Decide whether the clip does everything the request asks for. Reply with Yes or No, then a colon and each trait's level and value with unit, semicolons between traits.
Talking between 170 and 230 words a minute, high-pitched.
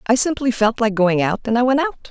No: fast, 285 wpm; high, 235 Hz